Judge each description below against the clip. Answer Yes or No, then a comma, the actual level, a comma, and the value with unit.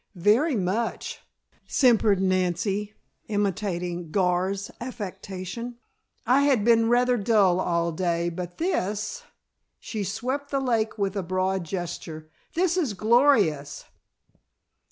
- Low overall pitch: No, high, 200 Hz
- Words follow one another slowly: Yes, slow, 115 wpm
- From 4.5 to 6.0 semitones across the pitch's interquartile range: Yes, average, 4.8 semitones